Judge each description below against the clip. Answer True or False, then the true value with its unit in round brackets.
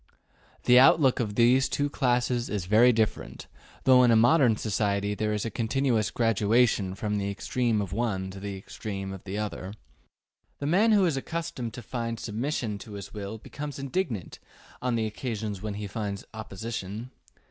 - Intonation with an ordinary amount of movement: True (3.5 semitones)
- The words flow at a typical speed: True (175 wpm)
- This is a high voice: False (110 Hz)